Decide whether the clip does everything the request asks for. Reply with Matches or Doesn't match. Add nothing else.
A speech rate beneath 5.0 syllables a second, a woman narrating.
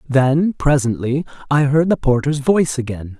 Doesn't match